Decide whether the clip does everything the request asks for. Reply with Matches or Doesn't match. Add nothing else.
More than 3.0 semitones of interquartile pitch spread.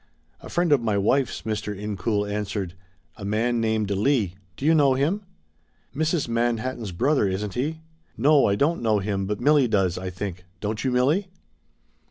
Matches